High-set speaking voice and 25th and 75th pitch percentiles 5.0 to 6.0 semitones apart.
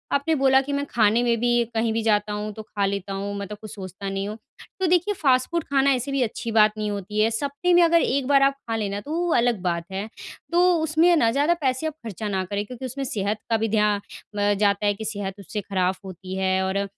Yes: high, 220 Hz; wide, 5.4 semitones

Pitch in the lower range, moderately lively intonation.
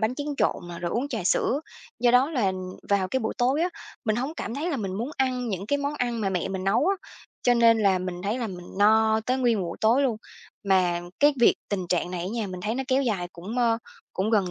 No: high, 225 Hz; average, 5.0 semitones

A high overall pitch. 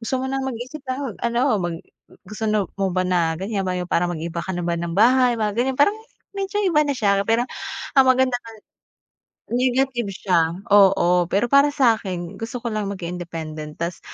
Yes: high, 210 Hz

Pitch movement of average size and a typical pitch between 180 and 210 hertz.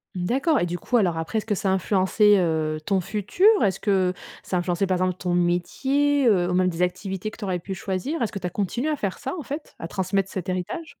Yes: average, 3.4 semitones; high, 190 Hz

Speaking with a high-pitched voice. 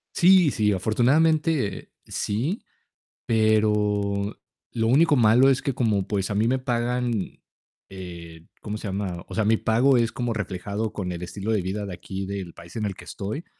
No: low, 105 Hz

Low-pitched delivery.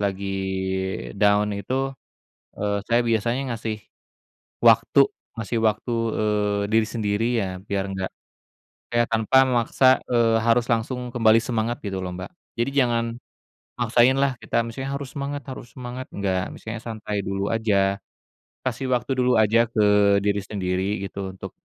Yes: low, 110 Hz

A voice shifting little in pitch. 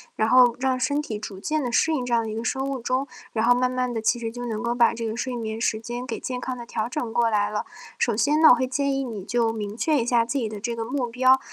Yes: narrow, 2.3 semitones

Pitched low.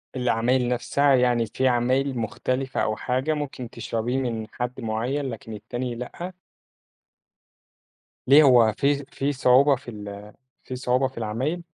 Yes: low, 125 Hz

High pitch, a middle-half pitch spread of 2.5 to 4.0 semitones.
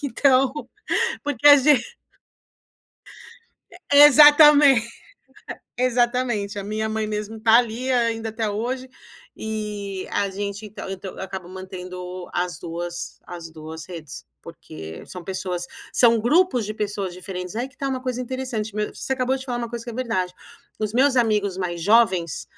No: high, 220 Hz; average, 5.2 semitones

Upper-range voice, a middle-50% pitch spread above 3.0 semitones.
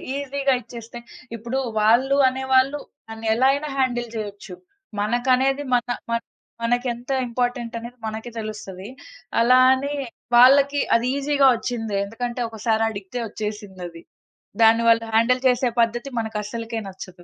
No: high, 235 Hz; average, 2.7 semitones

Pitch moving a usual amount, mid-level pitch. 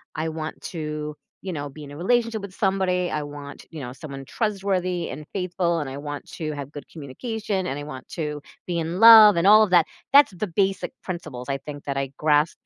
Yes: average, 4.7 semitones; medium, 165 Hz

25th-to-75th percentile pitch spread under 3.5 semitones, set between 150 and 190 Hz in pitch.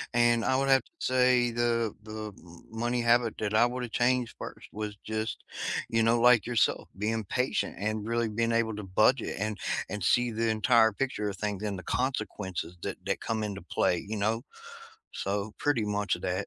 No: narrow, 2.4 semitones; low, 110 Hz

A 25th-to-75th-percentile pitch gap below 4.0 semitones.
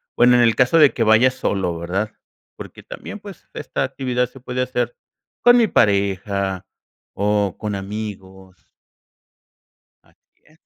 No: average, 4.5 semitones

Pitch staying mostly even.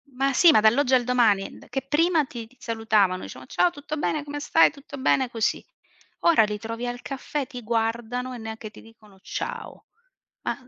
No: average, 4.3 semitones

